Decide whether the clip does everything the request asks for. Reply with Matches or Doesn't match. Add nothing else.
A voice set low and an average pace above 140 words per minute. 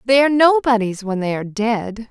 Doesn't match